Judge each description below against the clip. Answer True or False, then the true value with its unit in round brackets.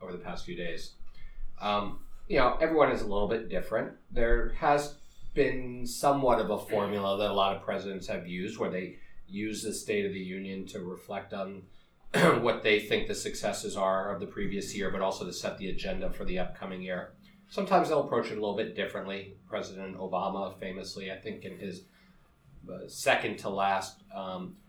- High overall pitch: False (100 Hz)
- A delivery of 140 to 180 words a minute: False (190 wpm)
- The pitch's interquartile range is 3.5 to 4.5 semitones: True (4.2 semitones)